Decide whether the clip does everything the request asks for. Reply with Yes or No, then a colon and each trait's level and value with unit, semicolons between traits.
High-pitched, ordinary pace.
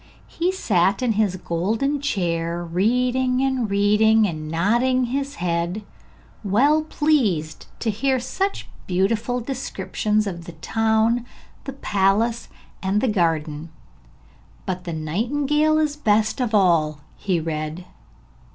No: high, 215 Hz; slow, 125 wpm